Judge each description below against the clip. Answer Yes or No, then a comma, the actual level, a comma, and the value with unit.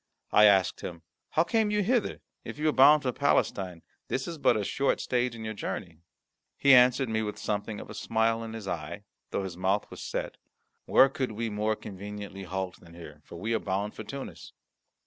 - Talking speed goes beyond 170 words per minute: Yes, fast, 205 wpm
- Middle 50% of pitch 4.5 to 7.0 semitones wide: Yes, average, 4.9 semitones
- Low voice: Yes, low, 110 Hz